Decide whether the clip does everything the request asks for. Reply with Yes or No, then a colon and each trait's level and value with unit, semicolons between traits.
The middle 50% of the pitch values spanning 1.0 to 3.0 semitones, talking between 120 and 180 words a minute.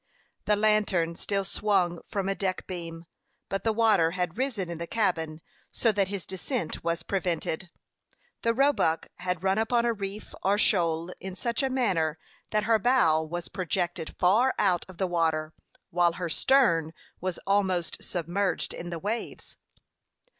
No: average, 3.9 semitones; average, 160 wpm